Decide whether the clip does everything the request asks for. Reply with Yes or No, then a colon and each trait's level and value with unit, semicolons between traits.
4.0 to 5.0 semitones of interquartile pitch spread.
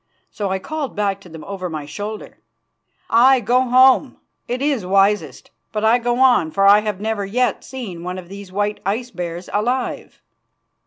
Yes: average, 4.6 semitones